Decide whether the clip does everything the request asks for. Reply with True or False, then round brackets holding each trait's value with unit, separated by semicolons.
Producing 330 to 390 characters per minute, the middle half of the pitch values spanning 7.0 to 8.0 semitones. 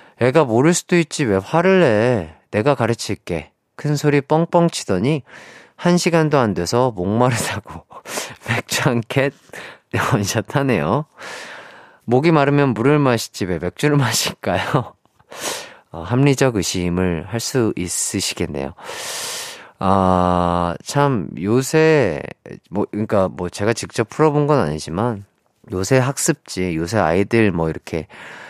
False (245 characters per minute; 7.5 semitones)